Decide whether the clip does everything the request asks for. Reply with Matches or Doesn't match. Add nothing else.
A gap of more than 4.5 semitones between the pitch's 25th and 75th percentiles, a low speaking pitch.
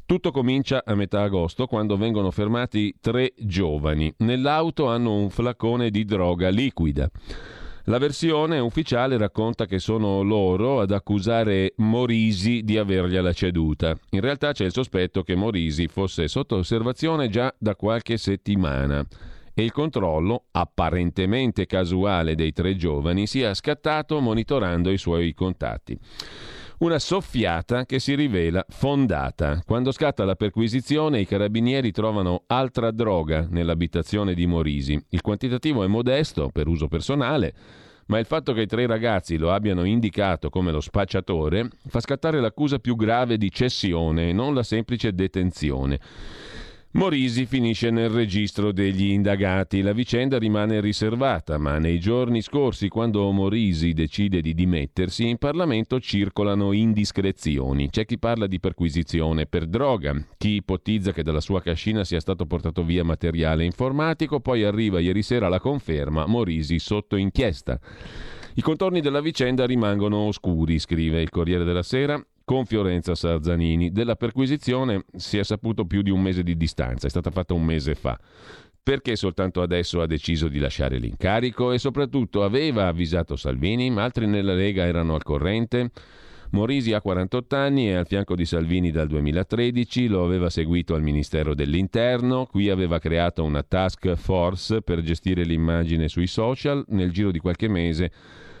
Matches